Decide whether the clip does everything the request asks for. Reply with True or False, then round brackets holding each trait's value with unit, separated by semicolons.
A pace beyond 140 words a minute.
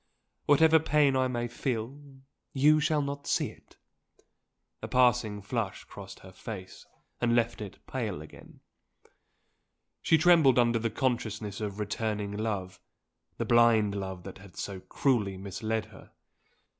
False (135 wpm)